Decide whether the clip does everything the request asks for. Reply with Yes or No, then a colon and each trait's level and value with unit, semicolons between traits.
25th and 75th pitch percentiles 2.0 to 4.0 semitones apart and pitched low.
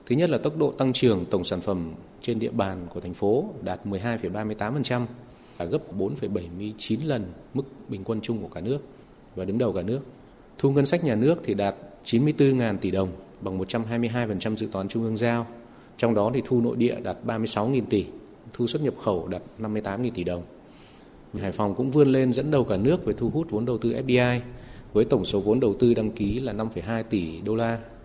Yes: average, 3.6 semitones; low, 115 Hz